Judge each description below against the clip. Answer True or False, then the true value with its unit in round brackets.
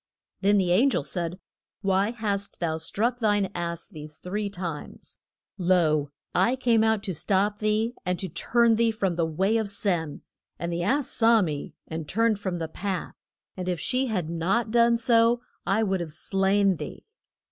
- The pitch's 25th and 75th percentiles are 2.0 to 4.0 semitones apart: False (4.4 semitones)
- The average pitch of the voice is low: False (195 Hz)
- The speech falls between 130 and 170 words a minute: False (180 wpm)